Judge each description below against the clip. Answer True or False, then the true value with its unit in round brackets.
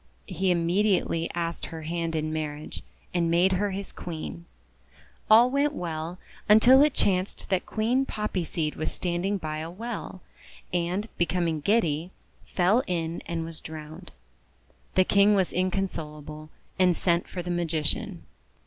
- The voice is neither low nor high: True (175 Hz)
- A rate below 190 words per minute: True (145 wpm)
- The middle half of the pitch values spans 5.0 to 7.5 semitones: False (3.4 semitones)